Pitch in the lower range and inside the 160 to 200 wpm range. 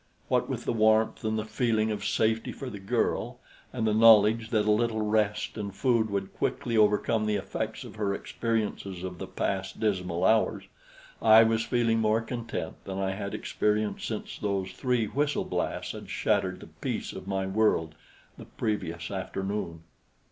Yes: low, 105 Hz; average, 170 wpm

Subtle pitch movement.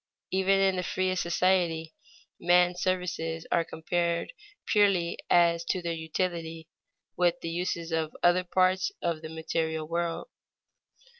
Yes: narrow, 1.9 semitones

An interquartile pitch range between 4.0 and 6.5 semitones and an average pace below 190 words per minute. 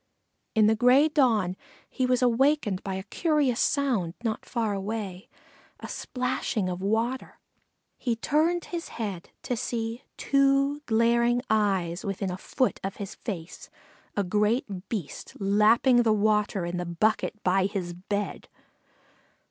Yes: average, 4.4 semitones; average, 140 wpm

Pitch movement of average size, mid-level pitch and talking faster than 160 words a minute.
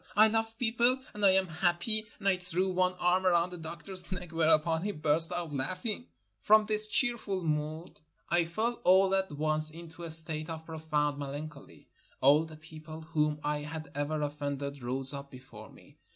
Yes: average, 3.7 semitones; medium, 165 Hz; average, 180 wpm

